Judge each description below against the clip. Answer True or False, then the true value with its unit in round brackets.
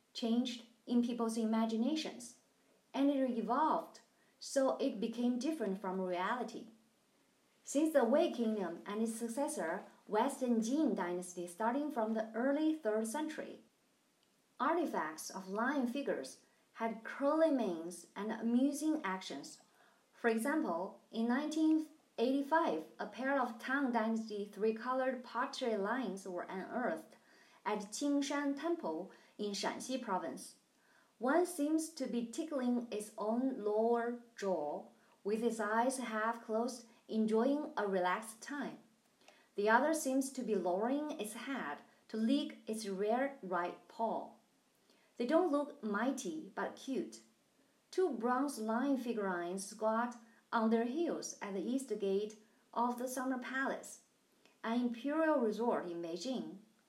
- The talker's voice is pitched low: False (235 Hz)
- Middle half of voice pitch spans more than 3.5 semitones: True (4.0 semitones)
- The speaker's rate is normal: False (125 wpm)